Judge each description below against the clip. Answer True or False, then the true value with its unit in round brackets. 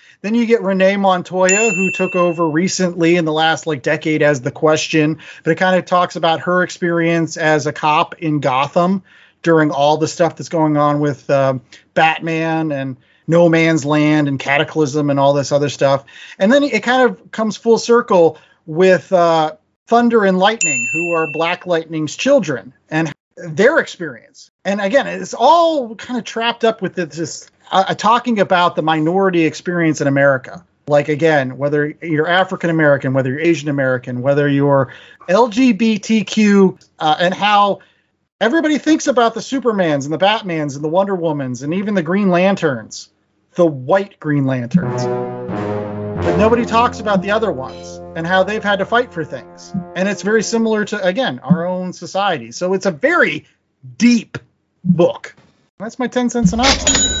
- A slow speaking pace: False (170 wpm)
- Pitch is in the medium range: True (170 Hz)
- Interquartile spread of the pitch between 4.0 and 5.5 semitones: True (4.7 semitones)